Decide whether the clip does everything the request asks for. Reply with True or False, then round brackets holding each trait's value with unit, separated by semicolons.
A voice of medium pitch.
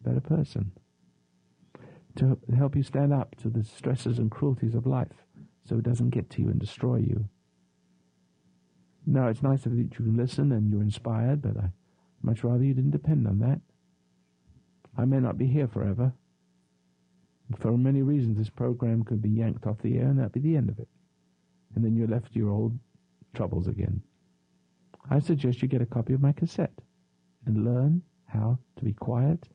False (115 Hz)